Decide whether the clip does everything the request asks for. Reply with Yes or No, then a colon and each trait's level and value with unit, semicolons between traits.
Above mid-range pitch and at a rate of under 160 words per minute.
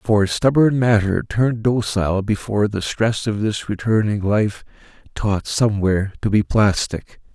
No: low, 105 Hz; average, 140 wpm